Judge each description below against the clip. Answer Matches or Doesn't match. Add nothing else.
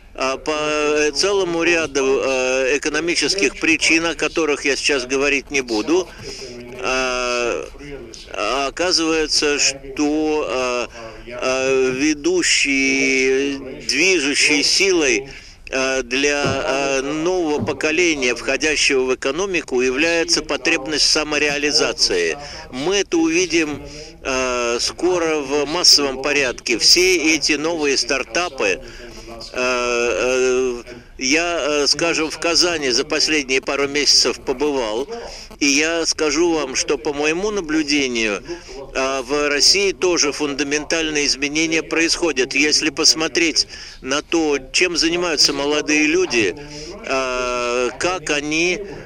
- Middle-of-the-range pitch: Matches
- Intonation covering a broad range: Doesn't match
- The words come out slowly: Matches